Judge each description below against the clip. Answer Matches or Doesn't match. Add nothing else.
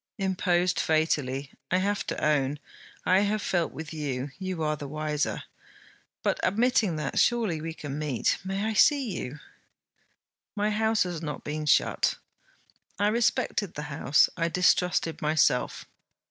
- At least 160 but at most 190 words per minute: Doesn't match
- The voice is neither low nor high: Matches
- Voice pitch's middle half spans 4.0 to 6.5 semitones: Matches